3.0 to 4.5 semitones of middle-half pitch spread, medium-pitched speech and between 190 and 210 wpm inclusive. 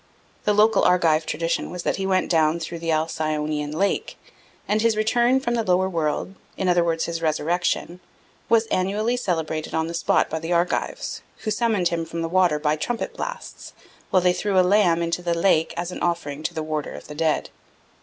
Yes: average, 3.3 semitones; medium, 170 Hz; average, 200 wpm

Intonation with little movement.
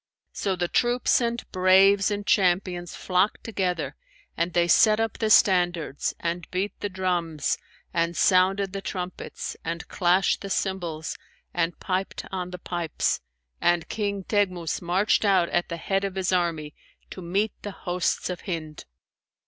Yes: narrow, 2.2 semitones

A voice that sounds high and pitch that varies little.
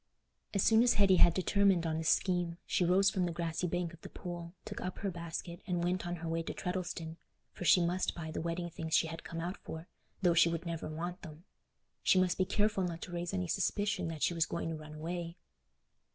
No: medium, 175 Hz; narrow, 1.8 semitones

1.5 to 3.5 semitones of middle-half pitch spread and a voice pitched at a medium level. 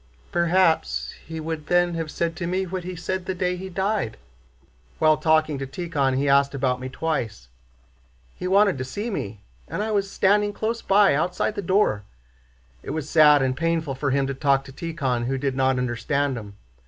No: wide, 5.4 semitones; medium, 155 Hz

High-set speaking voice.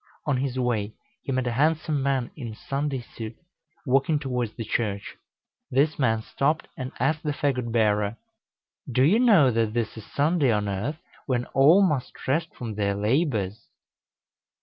No: low, 130 Hz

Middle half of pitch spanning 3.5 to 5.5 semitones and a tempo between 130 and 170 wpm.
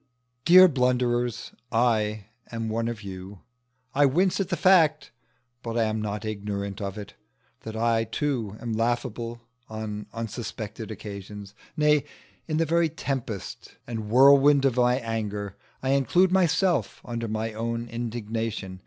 Yes: average, 4.0 semitones; average, 140 wpm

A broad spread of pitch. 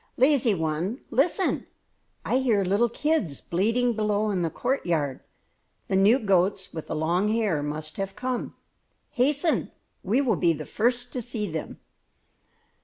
Yes: wide, 6.1 semitones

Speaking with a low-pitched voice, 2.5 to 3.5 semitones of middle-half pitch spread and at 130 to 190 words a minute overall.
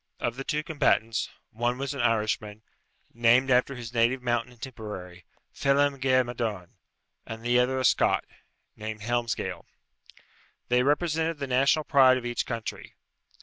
Yes: low, 120 Hz; average, 2.8 semitones; average, 145 wpm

